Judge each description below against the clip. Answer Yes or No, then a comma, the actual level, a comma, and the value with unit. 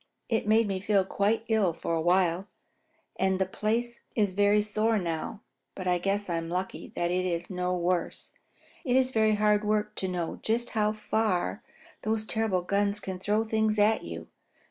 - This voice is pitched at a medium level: No, high, 205 Hz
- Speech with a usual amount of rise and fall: Yes, average, 3.0 semitones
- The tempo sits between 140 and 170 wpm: No, average, 180 wpm